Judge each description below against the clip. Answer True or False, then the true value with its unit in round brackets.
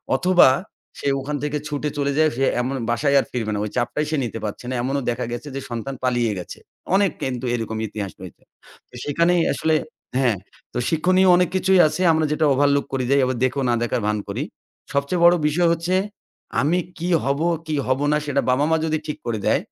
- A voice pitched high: False (140 Hz)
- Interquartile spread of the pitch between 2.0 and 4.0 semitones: False (4.4 semitones)